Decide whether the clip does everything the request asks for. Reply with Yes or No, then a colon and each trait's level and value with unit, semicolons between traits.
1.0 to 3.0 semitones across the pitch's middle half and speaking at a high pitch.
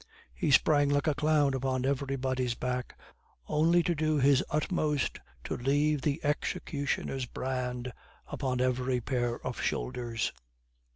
No: average, 2.7 semitones; low, 135 Hz